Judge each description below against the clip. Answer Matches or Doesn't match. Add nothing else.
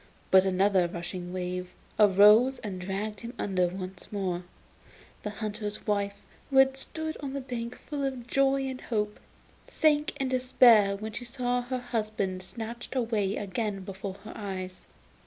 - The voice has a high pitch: Matches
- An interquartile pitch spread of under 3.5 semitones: Doesn't match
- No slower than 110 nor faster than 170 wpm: Matches